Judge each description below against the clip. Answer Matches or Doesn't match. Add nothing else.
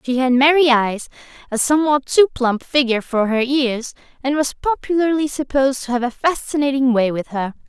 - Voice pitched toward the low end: Doesn't match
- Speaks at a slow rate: Doesn't match